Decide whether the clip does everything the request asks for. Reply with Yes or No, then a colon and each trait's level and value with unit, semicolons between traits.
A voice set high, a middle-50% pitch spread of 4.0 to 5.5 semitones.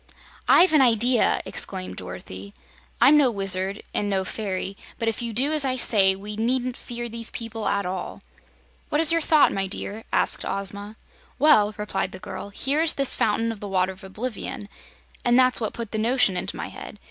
Yes: high, 220 Hz; average, 4.4 semitones